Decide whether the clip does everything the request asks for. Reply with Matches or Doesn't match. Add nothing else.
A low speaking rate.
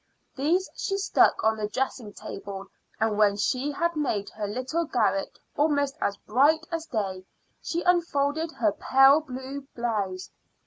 Doesn't match